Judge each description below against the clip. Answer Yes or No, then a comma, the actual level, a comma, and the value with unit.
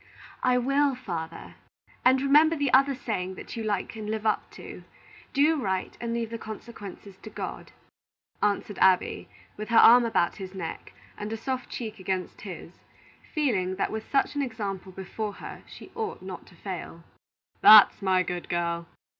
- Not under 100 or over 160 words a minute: No, average, 170 wpm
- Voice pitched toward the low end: No, high, 215 Hz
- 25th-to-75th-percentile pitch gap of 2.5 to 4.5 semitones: No, average, 4.9 semitones